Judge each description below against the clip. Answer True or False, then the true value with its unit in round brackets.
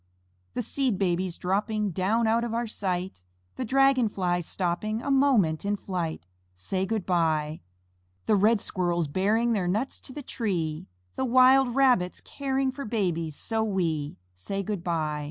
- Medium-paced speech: True (155 wpm)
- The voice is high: True (200 Hz)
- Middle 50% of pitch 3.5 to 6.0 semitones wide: True (5.1 semitones)